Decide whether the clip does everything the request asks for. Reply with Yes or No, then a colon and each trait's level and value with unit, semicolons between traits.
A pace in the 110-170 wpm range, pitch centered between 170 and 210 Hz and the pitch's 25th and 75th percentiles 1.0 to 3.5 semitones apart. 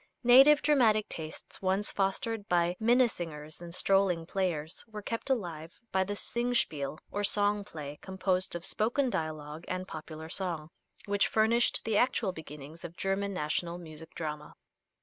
No: average, 145 wpm; medium, 185 Hz; average, 4.8 semitones